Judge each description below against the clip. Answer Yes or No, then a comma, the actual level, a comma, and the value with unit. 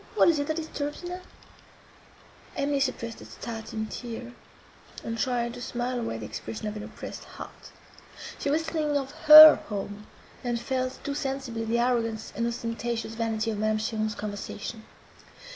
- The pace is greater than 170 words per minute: No, average, 160 wpm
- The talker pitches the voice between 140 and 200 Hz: No, high, 235 Hz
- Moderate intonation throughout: Yes, average, 3.8 semitones